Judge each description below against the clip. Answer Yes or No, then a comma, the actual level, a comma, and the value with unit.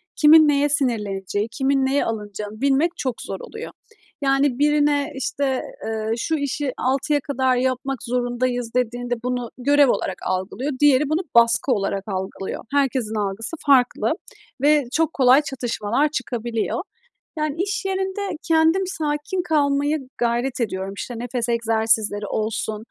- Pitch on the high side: Yes, very high, 260 Hz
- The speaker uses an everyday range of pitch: Yes, average, 4.2 semitones